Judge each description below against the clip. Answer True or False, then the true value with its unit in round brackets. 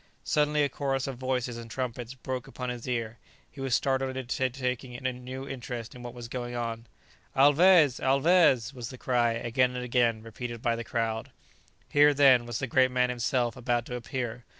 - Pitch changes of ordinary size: False (1.9 semitones)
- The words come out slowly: False (190 wpm)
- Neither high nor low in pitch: False (125 Hz)